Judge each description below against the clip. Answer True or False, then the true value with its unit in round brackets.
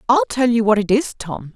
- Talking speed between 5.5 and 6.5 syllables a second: False (5.3 syllables/s)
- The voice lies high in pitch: True (225 Hz)